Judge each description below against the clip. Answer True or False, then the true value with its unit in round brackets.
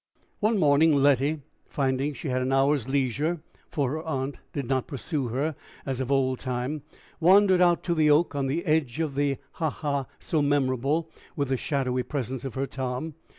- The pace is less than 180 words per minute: False (185 wpm)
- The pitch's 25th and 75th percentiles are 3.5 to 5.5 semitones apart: False (2.9 semitones)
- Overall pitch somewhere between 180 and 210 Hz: False (140 Hz)